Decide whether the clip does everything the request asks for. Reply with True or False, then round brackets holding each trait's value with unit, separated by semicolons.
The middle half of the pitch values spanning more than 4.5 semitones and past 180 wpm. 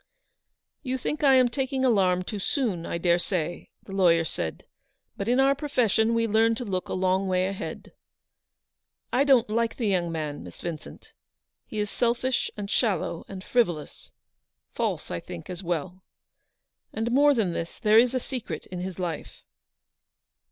False (5.5 semitones; 170 wpm)